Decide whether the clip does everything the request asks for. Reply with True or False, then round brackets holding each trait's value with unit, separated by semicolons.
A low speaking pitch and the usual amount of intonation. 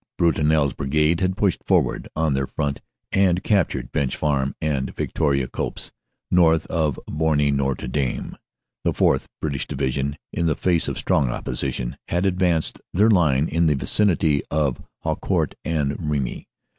True (75 Hz; 3.4 semitones)